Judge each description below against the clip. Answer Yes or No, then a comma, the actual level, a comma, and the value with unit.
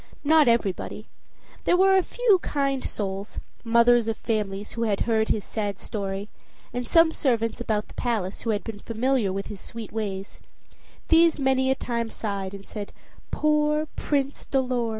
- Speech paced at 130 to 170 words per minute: Yes, average, 165 wpm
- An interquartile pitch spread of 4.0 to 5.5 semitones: Yes, average, 4.7 semitones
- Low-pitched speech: No, high, 230 Hz